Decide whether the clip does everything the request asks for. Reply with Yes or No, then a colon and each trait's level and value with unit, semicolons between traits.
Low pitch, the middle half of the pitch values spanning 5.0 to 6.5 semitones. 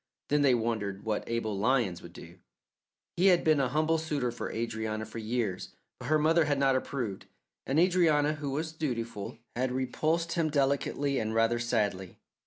Yes: low, 130 Hz; wide, 5.5 semitones